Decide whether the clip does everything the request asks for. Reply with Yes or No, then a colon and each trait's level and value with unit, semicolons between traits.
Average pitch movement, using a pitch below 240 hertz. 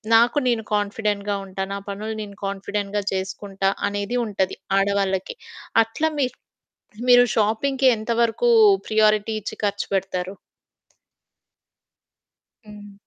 No: narrow, 2.0 semitones; high, 205 Hz